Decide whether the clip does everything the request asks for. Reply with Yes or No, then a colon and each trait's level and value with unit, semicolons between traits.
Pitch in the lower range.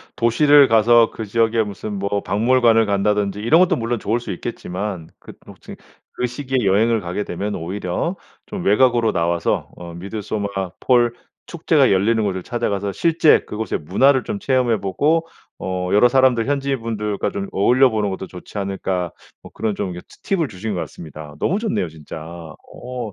Yes: low, 110 Hz